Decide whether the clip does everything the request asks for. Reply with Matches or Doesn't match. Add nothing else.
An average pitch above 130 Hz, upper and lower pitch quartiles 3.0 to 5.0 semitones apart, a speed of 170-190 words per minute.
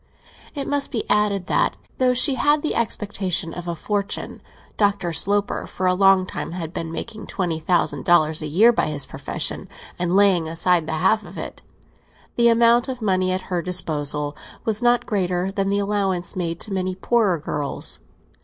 Matches